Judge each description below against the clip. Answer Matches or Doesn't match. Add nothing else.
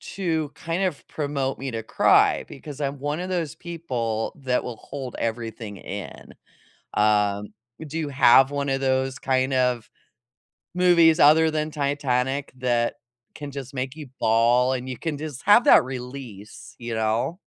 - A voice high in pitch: Doesn't match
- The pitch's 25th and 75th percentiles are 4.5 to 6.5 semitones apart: Doesn't match